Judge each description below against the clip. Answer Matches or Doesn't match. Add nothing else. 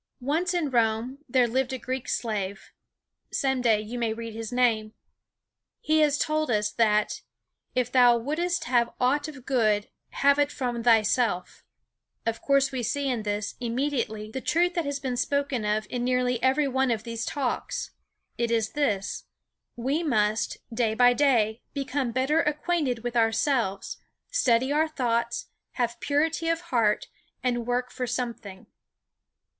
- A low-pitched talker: Doesn't match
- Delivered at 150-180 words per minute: Matches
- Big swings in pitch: Doesn't match